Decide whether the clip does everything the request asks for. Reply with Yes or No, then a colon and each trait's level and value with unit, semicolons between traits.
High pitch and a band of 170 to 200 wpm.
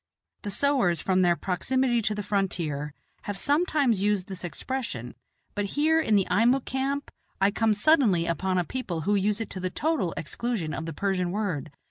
Yes: high, 200 Hz; average, 180 wpm